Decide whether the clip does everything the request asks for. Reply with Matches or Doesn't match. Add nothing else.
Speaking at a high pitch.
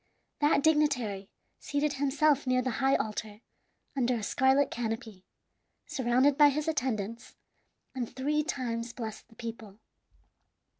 Matches